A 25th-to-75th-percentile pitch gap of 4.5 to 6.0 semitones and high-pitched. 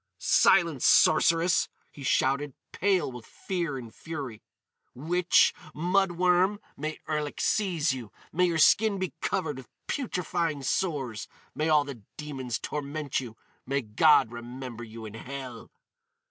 No: average, 5.2 semitones; medium, 150 Hz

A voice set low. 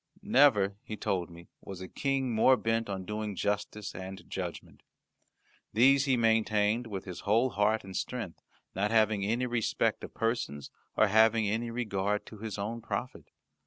Yes: low, 110 Hz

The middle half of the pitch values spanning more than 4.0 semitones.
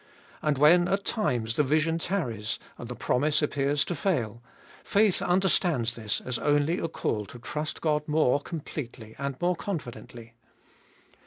Yes: wide, 5.6 semitones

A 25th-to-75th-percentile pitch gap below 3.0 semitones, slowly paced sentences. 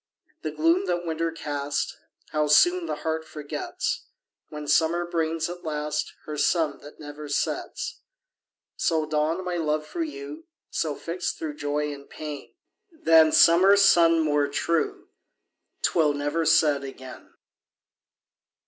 Yes: narrow, 2.4 semitones; slow, 130 wpm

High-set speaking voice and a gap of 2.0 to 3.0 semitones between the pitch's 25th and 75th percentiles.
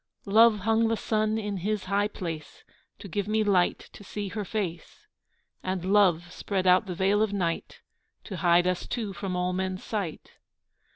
Yes: high, 195 Hz; average, 2.7 semitones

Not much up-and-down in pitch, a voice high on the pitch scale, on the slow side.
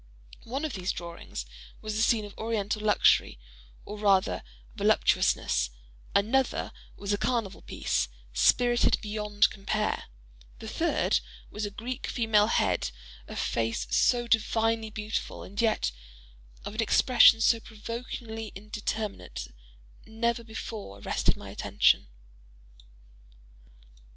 Yes: narrow, 2.3 semitones; high, 215 Hz; slow, 110 wpm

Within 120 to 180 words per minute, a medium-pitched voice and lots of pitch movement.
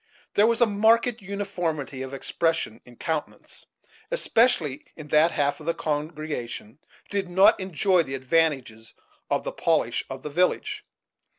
Yes: average, 150 wpm; medium, 160 Hz; wide, 5.9 semitones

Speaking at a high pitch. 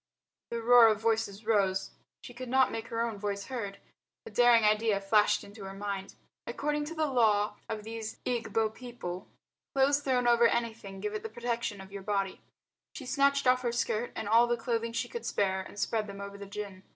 Yes: high, 225 Hz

